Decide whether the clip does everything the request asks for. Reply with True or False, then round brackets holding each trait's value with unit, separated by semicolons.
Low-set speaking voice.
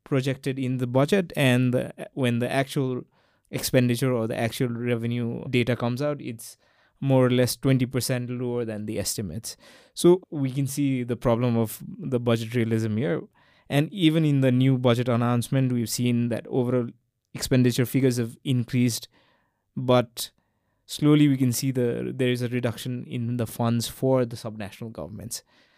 True (125 Hz)